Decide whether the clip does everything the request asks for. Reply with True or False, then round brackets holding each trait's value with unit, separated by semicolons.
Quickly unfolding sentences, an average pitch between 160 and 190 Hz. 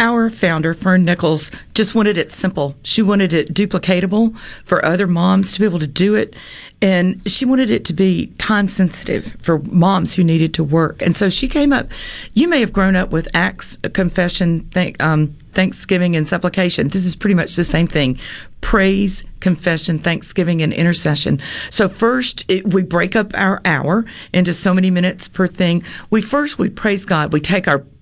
False (185 wpm; 185 Hz)